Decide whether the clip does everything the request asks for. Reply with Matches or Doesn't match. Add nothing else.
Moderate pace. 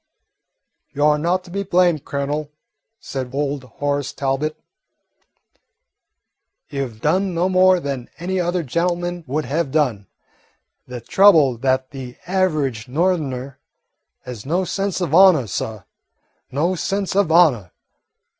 Doesn't match